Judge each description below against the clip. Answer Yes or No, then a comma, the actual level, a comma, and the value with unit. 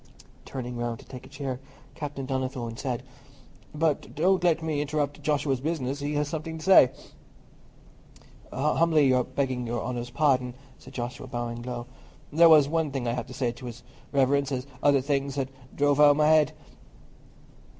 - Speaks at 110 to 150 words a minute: No, average, 165 wpm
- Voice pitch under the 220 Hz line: Yes, medium, 140 Hz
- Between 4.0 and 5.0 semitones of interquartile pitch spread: No, average, 3.1 semitones